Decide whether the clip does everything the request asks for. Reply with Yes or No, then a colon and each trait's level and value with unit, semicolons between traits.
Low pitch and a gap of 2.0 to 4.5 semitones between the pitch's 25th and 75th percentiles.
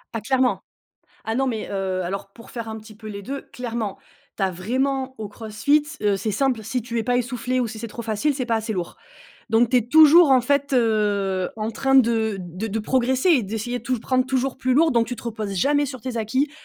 No: high, 235 Hz; average, 3.4 semitones